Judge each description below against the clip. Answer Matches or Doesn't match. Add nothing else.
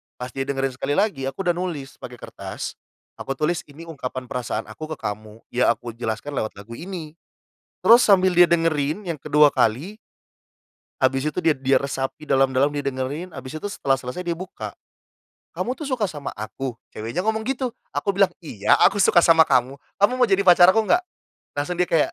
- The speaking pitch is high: Doesn't match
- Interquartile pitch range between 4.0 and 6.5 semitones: Matches